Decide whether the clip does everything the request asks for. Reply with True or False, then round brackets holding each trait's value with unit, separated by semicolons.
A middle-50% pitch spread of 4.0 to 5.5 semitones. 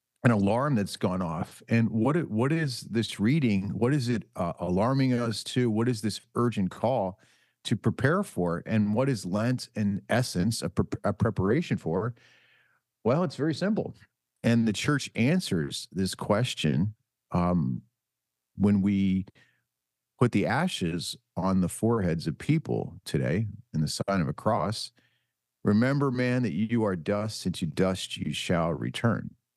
True (4.8 semitones)